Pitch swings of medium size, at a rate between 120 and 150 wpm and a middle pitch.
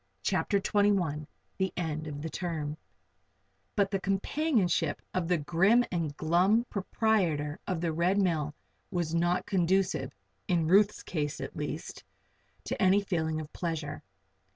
Yes: average, 3.7 semitones; slow, 135 wpm; medium, 175 Hz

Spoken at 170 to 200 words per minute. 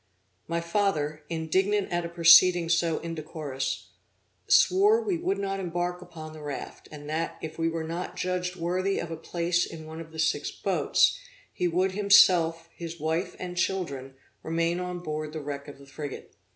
Yes: average, 175 wpm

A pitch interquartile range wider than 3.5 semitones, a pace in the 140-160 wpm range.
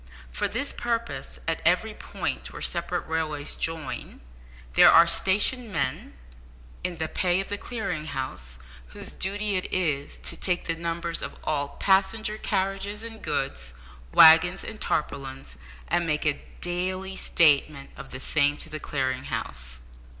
Yes: average, 5.2 semitones; average, 150 wpm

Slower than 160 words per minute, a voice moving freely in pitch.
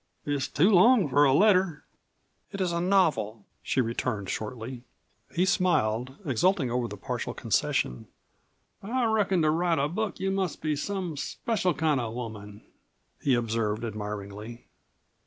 Yes: average, 150 wpm; wide, 8.2 semitones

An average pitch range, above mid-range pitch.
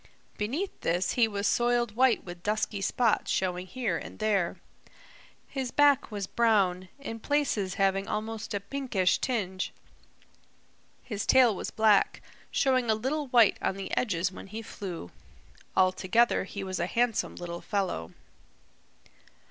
Yes: average, 4.2 semitones; high, 210 Hz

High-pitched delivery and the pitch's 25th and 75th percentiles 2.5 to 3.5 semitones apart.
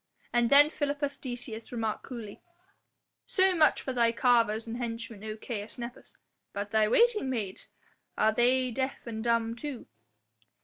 Yes: high, 235 Hz; average, 2.9 semitones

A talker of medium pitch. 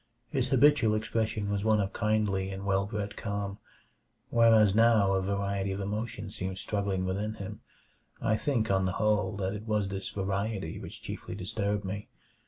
No: low, 100 Hz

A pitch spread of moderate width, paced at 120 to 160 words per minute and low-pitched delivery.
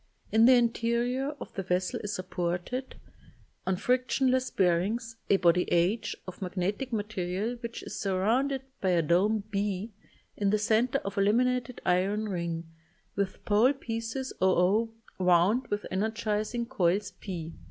No: average, 4.2 semitones; average, 140 wpm; high, 210 Hz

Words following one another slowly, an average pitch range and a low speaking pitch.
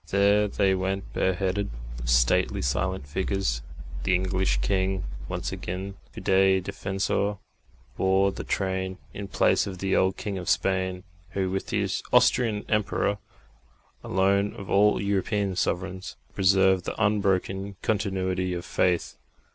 No: slow, 130 wpm; narrow, 1.2 semitones; very low, 95 Hz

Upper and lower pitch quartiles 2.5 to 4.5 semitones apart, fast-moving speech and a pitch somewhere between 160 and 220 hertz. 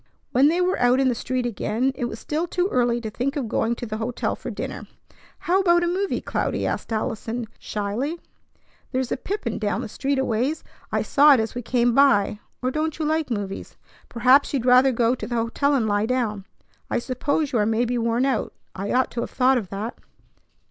No: average, 3.6 semitones; fast, 215 wpm; high, 245 Hz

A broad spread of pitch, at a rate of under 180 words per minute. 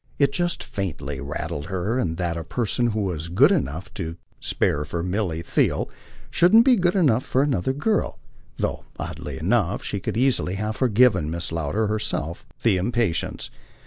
Yes: wide, 7.2 semitones; average, 170 wpm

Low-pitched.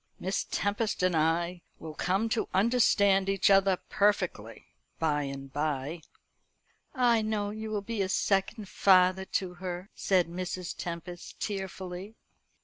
No: high, 190 Hz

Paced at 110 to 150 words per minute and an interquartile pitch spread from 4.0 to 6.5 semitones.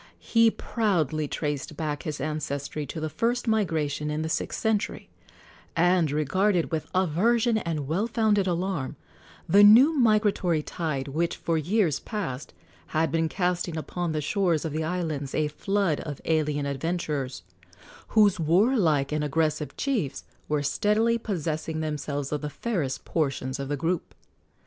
Yes: average, 145 wpm; average, 5.0 semitones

